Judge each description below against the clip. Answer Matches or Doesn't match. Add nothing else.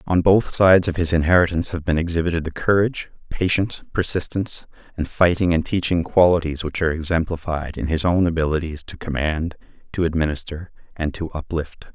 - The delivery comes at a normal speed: Matches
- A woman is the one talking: Doesn't match